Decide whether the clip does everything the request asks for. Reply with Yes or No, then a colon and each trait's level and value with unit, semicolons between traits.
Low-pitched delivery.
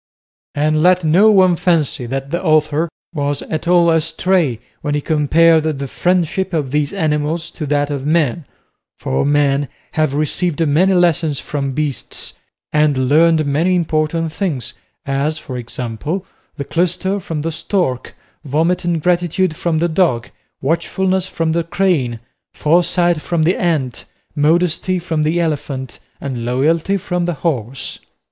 No: medium, 155 Hz